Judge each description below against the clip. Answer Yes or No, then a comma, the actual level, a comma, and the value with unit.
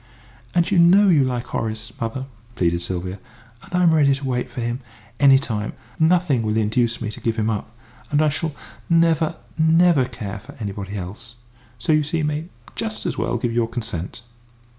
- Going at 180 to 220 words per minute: Yes, average, 190 wpm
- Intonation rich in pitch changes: Yes, wide, 6.3 semitones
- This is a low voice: Yes, low, 125 Hz